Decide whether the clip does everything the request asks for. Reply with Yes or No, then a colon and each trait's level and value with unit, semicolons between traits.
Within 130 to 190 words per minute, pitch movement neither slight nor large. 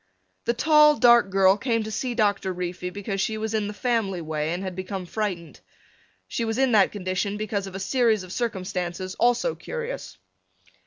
Yes: average, 180 wpm; average, 3.9 semitones